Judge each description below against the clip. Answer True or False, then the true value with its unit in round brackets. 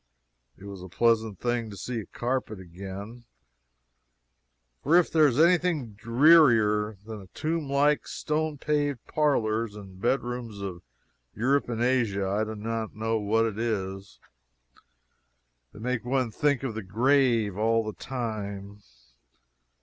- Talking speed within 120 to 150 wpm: True (145 wpm)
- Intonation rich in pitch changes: False (4.2 semitones)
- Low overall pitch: True (115 Hz)